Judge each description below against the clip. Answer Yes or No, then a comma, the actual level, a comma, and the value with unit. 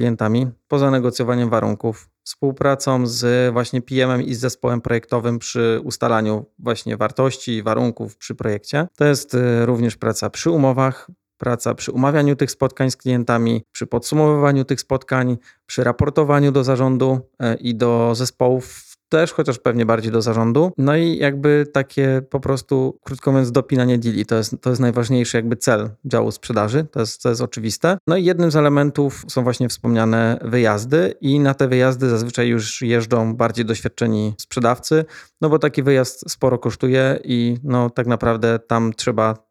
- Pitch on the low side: Yes, low, 125 Hz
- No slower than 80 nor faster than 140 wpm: No, average, 155 wpm